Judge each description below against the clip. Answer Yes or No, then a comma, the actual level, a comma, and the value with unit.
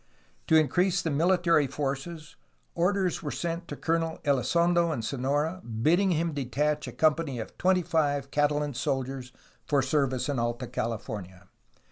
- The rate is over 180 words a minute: No, average, 140 wpm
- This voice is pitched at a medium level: Yes, medium, 150 Hz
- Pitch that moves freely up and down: No, average, 4.0 semitones